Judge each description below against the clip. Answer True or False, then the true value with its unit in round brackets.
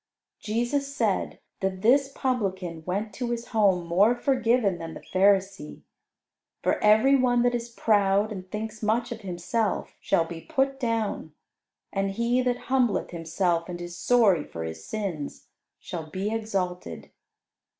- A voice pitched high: True (210 Hz)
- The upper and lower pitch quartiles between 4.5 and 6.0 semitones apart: True (4.9 semitones)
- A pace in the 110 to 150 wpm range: True (145 wpm)